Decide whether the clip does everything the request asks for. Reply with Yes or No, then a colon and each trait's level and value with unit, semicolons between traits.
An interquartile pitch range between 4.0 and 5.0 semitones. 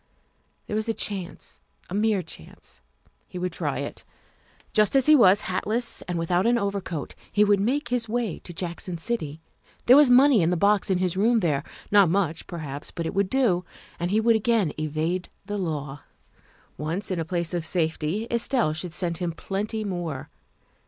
Yes: average, 4.6 semitones